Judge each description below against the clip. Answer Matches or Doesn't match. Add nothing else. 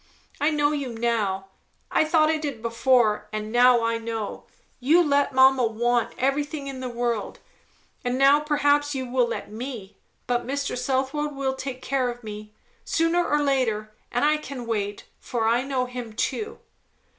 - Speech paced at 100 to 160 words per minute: Doesn't match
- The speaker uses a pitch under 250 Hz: Doesn't match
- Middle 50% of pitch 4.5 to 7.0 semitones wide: Doesn't match